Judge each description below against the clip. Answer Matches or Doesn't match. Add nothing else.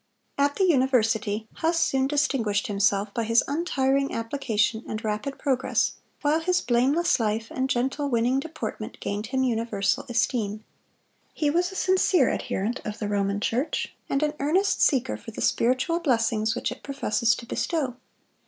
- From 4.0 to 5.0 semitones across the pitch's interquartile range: Matches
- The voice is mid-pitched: Doesn't match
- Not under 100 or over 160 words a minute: Matches